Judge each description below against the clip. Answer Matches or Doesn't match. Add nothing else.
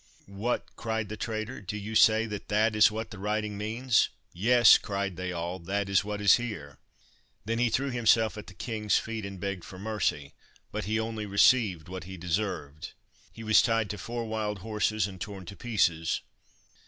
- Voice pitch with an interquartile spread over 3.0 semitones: Doesn't match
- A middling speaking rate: Matches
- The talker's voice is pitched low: Matches